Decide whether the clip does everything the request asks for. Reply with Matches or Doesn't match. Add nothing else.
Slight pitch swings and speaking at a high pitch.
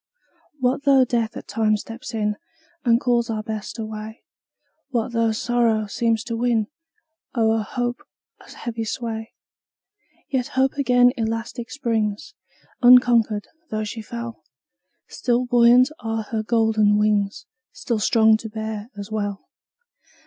Matches